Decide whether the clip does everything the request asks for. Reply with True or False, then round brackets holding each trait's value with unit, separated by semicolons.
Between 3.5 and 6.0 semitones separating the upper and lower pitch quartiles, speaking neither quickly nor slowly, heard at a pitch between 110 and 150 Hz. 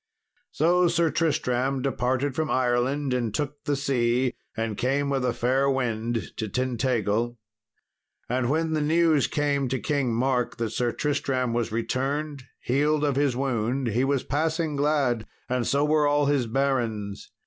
False (3.1 semitones; 155 wpm; 135 Hz)